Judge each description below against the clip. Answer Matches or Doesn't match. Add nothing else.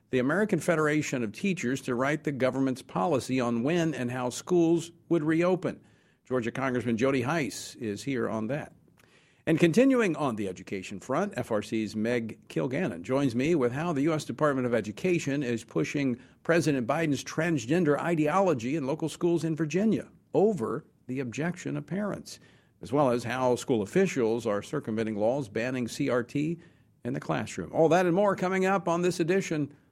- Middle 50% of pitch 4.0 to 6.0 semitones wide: Matches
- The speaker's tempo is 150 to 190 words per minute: Matches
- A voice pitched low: Doesn't match